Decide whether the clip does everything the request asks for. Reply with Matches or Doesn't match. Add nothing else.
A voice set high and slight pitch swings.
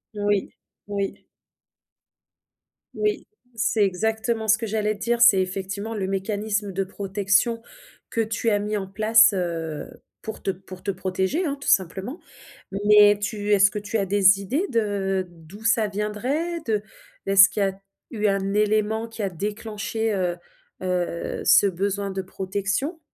Matches